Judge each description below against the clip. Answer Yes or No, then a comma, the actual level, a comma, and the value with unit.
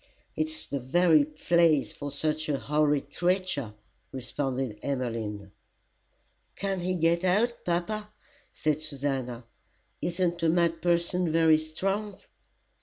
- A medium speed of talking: No, slow, 110 wpm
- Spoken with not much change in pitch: No, average, 4.0 semitones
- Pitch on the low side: No, medium, 155 Hz